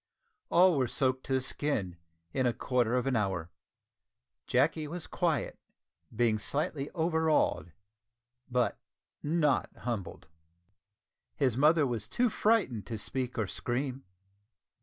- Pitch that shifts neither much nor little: Yes, average, 4.5 semitones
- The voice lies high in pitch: No, low, 130 Hz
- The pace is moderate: No, slow, 120 wpm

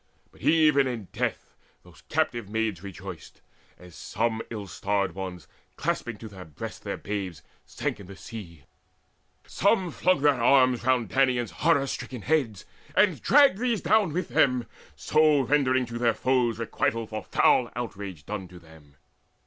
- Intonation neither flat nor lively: No, wide, 6.0 semitones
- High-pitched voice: No, low, 115 Hz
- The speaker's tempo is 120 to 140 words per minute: No, average, 155 wpm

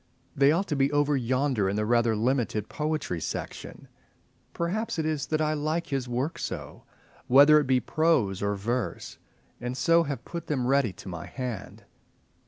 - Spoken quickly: No, average, 175 wpm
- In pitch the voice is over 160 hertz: No, low, 135 Hz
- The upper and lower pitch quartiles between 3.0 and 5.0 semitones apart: Yes, average, 4.6 semitones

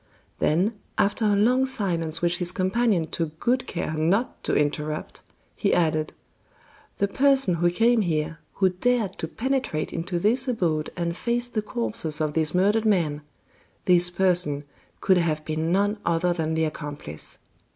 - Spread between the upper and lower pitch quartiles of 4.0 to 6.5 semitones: Yes, average, 5.2 semitones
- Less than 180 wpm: Yes, average, 155 wpm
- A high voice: No, medium, 180 Hz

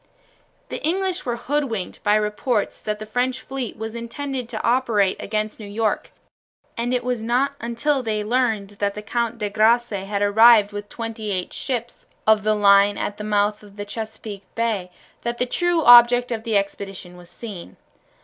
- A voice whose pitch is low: No, high, 220 Hz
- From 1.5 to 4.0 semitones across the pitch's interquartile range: Yes, average, 2.8 semitones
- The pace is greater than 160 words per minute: Yes, average, 180 wpm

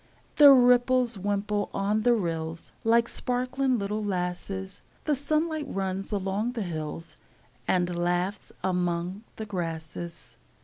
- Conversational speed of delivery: No, slow, 120 wpm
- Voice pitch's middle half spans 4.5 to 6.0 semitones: Yes, wide, 5.4 semitones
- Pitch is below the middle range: No, high, 200 Hz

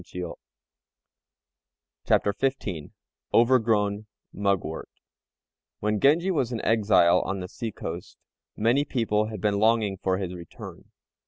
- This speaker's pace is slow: Yes, slow, 115 wpm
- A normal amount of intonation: Yes, average, 3.3 semitones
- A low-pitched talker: Yes, low, 105 Hz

